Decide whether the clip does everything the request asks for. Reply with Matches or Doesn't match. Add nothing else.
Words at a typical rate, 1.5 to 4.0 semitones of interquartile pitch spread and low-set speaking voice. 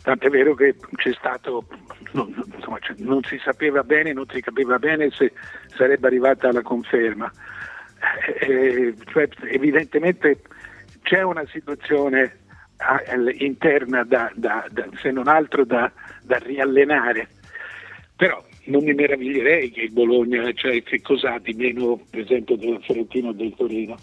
Matches